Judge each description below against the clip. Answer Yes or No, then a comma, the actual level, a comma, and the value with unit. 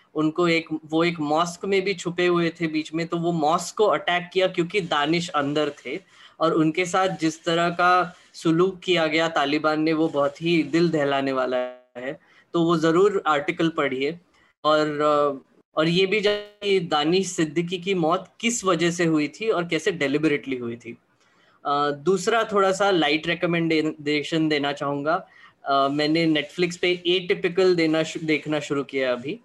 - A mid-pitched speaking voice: Yes, medium, 165 Hz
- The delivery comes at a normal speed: Yes, average, 165 wpm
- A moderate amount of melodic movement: Yes, average, 3.2 semitones